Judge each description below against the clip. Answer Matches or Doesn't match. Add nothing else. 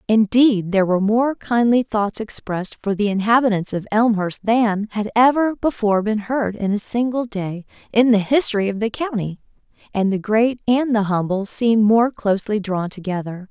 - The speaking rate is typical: Matches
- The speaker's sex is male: Doesn't match